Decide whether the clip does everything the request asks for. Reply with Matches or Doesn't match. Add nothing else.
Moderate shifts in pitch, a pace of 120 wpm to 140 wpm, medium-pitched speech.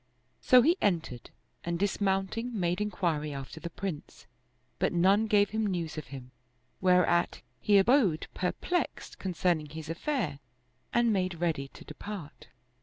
Matches